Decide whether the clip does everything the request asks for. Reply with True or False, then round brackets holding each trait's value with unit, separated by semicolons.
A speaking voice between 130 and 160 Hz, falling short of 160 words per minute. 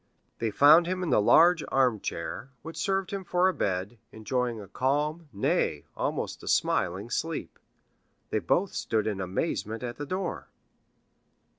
True (135 Hz; 150 wpm)